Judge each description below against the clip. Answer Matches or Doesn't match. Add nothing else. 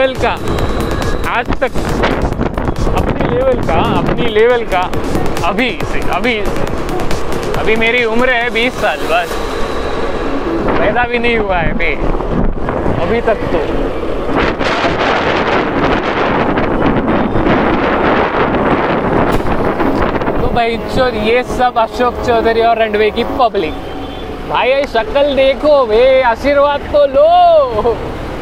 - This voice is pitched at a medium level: Doesn't match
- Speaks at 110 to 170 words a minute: Doesn't match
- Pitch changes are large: Doesn't match